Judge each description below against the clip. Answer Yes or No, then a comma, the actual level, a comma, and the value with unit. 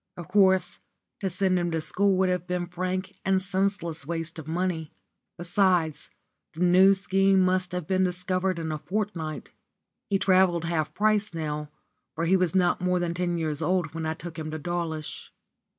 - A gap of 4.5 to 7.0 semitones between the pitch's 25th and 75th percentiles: No, narrow, 2.4 semitones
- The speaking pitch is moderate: Yes, medium, 180 Hz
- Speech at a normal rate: Yes, average, 180 wpm